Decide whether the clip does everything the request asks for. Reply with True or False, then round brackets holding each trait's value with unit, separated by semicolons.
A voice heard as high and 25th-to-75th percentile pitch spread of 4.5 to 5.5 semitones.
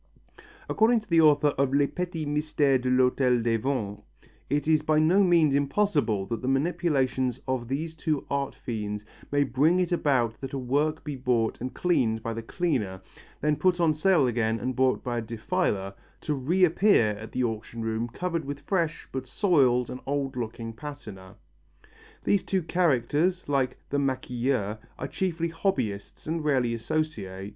False (135 Hz; 5.1 semitones)